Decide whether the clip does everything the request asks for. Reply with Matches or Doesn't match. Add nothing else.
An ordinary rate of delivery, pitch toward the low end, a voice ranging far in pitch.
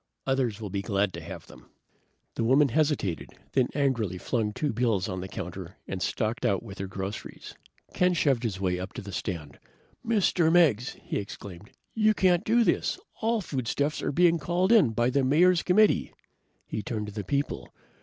Matches